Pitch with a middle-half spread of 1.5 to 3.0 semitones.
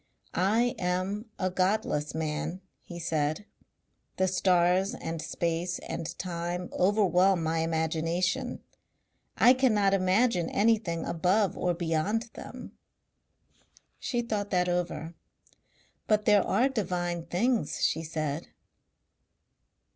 No: average, 3.8 semitones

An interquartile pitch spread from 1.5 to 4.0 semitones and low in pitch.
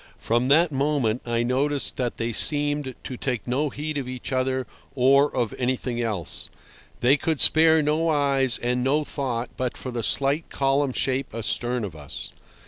Yes: average, 2.9 semitones; low, 130 Hz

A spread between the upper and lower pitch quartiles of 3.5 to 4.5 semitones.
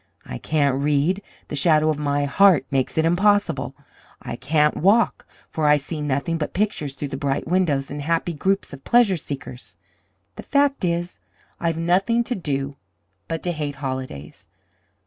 Yes: average, 4.2 semitones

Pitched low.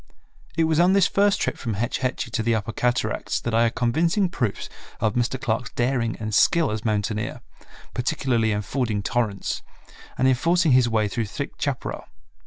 Yes: low, 120 Hz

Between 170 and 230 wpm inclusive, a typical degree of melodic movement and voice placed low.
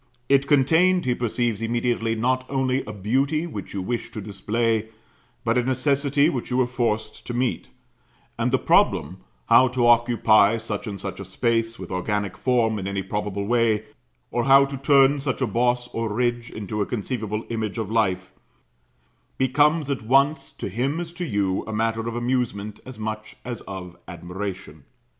Yes: average, 175 wpm; average, 3.6 semitones; low, 115 Hz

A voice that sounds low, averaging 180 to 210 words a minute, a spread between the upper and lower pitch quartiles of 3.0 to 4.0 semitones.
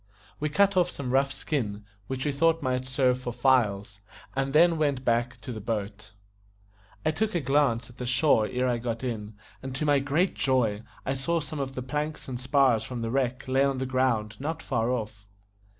Yes: low, 130 Hz; average, 200 wpm; average, 3.3 semitones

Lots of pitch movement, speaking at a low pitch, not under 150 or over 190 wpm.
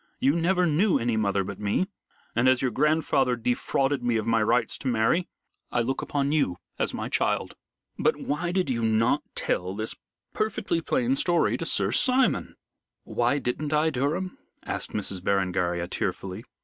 Yes: wide, 5.8 semitones; low, 125 Hz; average, 165 wpm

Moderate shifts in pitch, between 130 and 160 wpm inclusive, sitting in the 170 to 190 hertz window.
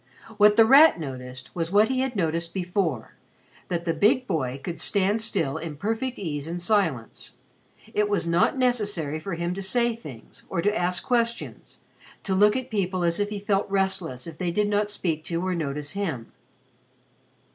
No: average, 4.2 semitones; average, 180 wpm; medium, 185 Hz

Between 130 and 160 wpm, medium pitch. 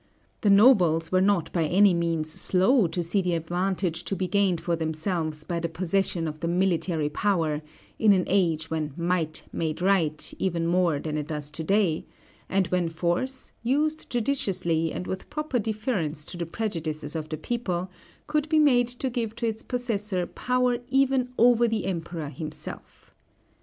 No: average, 170 wpm; medium, 180 Hz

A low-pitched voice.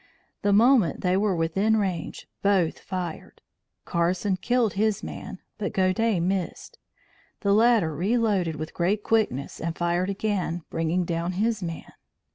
No: high, 190 Hz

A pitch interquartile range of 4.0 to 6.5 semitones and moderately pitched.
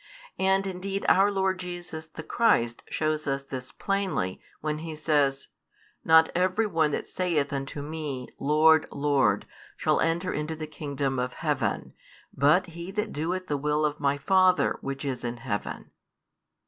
Yes: average, 4.5 semitones; medium, 155 Hz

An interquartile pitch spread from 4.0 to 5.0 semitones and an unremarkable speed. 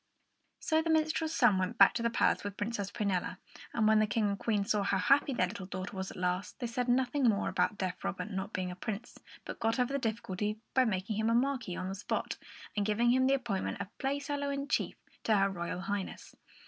No: average, 4.4 semitones; fast, 230 wpm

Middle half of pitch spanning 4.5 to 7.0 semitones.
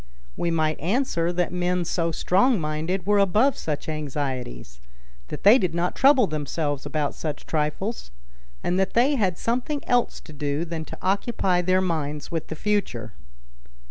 Yes: average, 4.9 semitones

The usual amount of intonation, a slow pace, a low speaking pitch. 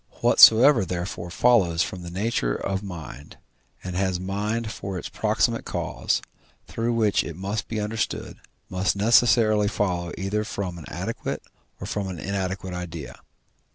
No: average, 3.3 semitones; average, 145 wpm; very low, 95 Hz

